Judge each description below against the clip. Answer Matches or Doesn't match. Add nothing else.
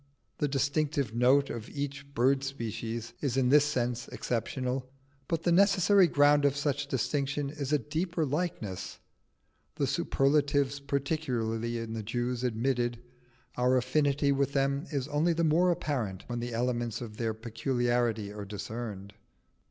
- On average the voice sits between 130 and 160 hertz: Matches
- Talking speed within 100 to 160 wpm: Matches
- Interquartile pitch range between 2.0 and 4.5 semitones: Matches